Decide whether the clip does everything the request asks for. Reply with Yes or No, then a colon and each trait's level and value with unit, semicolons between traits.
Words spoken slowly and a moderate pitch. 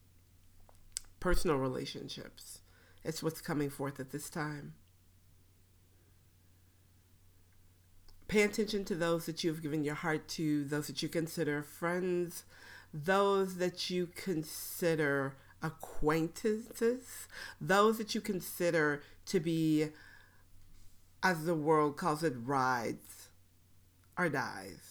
Yes: slow, 105 wpm; medium, 150 Hz